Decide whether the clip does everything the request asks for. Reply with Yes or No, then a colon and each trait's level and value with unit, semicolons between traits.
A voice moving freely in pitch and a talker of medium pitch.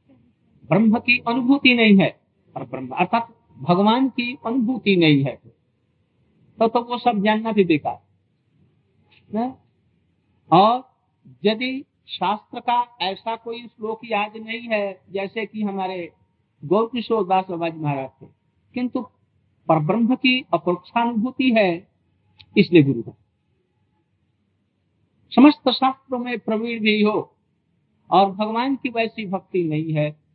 No: wide, 7.7 semitones; high, 205 Hz